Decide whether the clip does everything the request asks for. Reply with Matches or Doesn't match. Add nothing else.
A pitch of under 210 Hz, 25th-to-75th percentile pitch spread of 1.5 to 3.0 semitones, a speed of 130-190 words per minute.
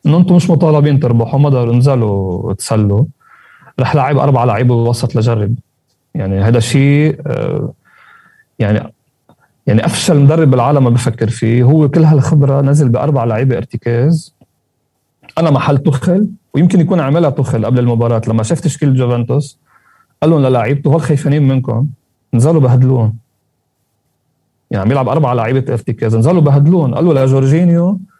Doesn't match